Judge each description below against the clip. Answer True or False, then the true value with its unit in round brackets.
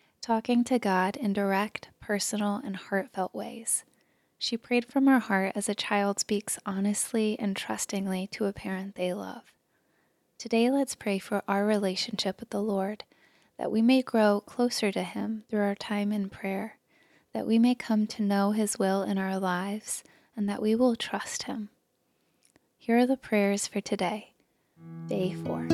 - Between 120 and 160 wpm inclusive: False (170 wpm)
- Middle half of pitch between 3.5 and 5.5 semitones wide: False (2.7 semitones)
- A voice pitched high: True (205 Hz)